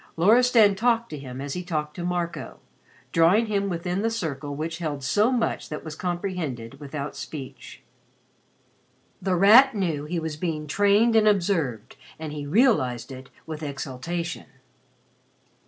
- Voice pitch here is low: No, medium, 170 Hz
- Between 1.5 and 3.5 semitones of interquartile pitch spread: No, wide, 5.5 semitones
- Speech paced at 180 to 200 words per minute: No, average, 150 wpm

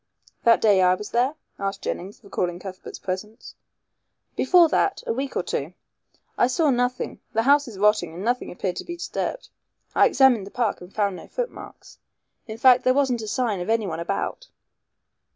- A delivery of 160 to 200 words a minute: Yes, average, 180 wpm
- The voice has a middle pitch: No, high, 225 Hz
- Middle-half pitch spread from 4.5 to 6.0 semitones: Yes, average, 4.9 semitones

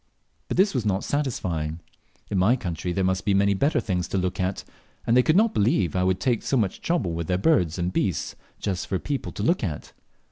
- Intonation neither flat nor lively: No, wide, 5.7 semitones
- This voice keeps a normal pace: No, fast, 225 wpm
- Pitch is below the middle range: Yes, very low, 95 Hz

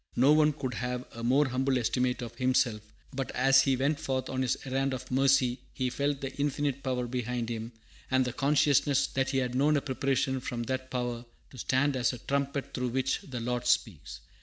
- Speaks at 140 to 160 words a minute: No, fast, 205 wpm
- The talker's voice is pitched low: Yes, low, 130 Hz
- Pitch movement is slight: Yes, narrow, 1.8 semitones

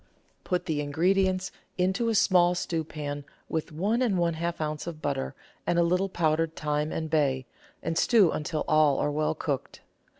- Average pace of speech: Yes, average, 170 wpm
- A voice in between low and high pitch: Yes, medium, 165 Hz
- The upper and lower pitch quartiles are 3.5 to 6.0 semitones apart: No, average, 3.1 semitones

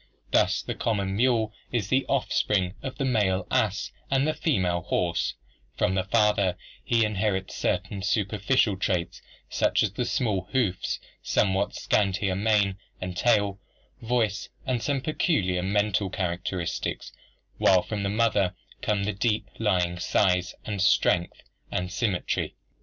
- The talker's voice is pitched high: No, low, 100 Hz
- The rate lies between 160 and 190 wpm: No, slow, 135 wpm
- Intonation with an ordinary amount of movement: Yes, average, 3.2 semitones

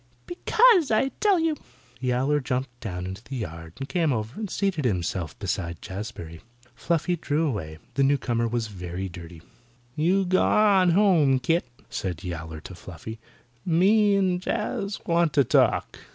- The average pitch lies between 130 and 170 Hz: Yes, low, 135 Hz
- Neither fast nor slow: Yes, average, 150 wpm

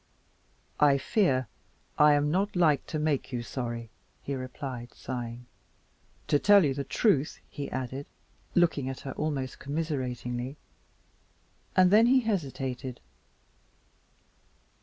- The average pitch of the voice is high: No, medium, 140 Hz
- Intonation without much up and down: No, average, 3.6 semitones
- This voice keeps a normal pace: No, slow, 115 wpm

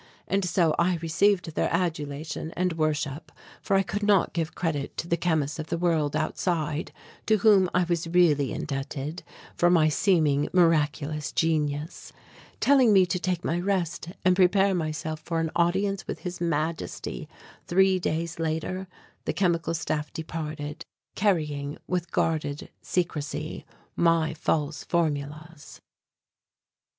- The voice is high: No, medium, 165 Hz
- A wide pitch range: No, average, 2.8 semitones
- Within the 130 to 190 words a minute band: Yes, slow, 135 wpm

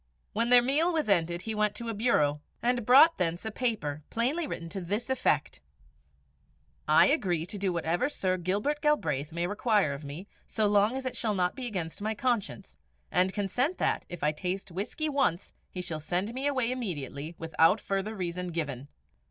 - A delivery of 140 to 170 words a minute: No, average, 185 wpm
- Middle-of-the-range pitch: No, high, 200 Hz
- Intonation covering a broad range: Yes, wide, 6.1 semitones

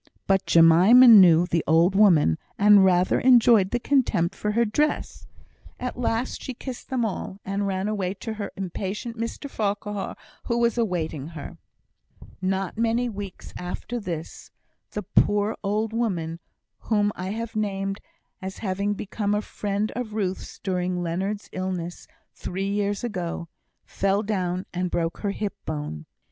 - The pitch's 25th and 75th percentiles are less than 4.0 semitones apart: Yes, average, 3.1 semitones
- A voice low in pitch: No, high, 200 Hz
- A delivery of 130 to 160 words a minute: Yes, average, 150 wpm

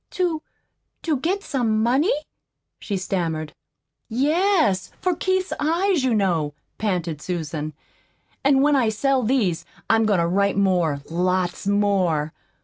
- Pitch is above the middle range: Yes, high, 210 Hz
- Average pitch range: No, wide, 8.3 semitones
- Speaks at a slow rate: Yes, slow, 130 wpm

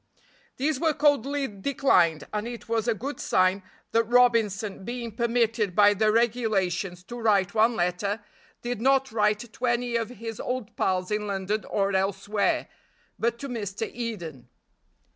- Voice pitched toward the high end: Yes, high, 220 Hz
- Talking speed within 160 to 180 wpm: No, average, 150 wpm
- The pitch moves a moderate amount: Yes, average, 3.3 semitones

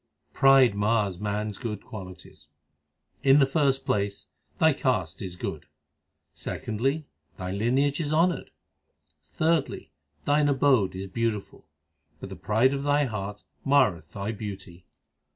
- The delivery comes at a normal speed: No, slow, 130 wpm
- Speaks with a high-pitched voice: No, low, 110 Hz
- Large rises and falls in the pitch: Yes, wide, 5.8 semitones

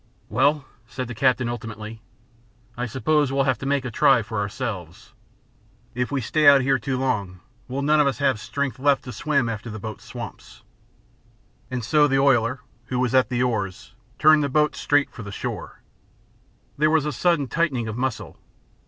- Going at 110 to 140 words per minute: No, average, 185 wpm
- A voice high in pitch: No, low, 130 Hz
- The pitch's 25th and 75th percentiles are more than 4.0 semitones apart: No, average, 3.7 semitones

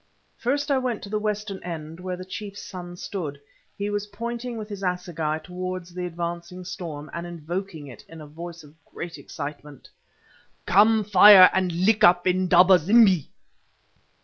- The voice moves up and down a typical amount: Yes, average, 3.2 semitones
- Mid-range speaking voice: Yes, medium, 180 Hz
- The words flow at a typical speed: Yes, average, 160 wpm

